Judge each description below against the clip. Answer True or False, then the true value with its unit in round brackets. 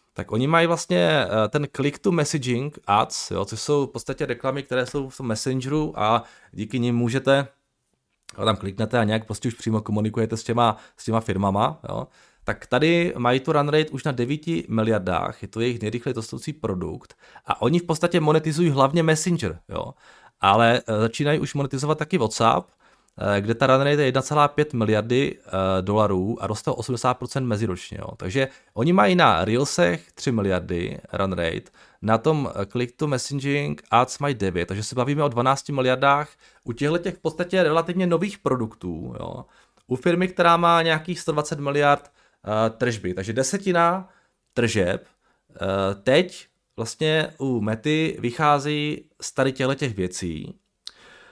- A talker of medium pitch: False (130 Hz)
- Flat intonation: False (5.4 semitones)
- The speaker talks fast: False (160 wpm)